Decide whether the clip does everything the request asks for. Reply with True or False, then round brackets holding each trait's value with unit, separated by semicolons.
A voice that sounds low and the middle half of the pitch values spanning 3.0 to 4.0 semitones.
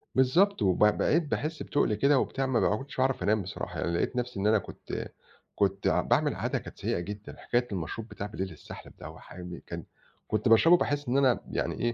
False (115 Hz; 5.0 semitones)